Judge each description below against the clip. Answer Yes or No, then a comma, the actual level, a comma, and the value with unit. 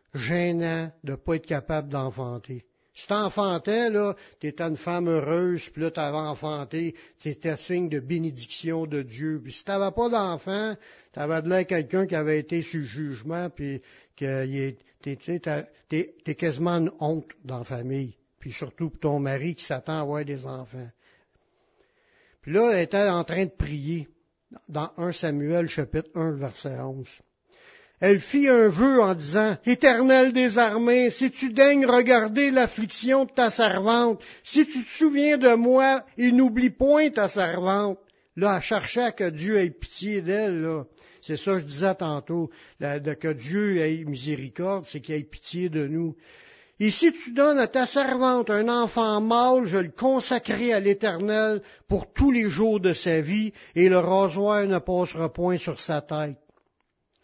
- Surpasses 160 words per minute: Yes, average, 170 wpm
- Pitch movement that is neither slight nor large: No, wide, 6.3 semitones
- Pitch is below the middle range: No, medium, 175 Hz